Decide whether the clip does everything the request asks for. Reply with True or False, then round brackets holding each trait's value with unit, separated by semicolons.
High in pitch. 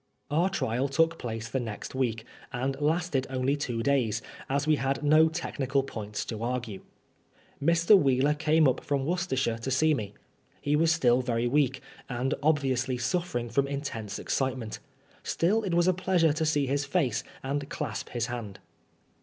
False (135 Hz)